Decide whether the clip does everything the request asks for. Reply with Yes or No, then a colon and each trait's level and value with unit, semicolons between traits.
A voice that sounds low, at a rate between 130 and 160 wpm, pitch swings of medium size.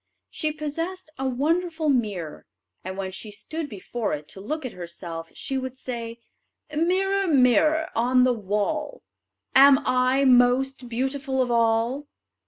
No: very high, 255 Hz; average, 140 wpm; average, 4.9 semitones